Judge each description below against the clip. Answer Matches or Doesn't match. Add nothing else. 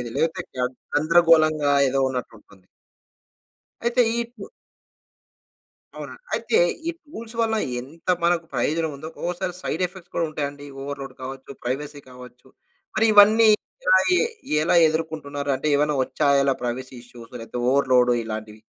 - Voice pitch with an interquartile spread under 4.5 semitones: Doesn't match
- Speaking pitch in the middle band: Matches